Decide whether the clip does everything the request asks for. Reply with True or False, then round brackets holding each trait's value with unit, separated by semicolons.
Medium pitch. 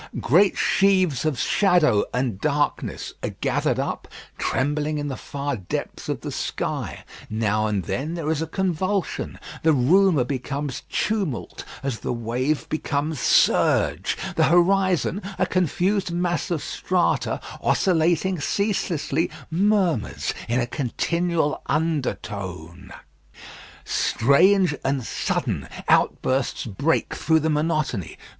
True (155 Hz)